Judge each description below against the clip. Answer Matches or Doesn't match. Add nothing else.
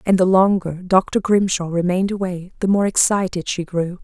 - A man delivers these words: Doesn't match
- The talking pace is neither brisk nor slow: Matches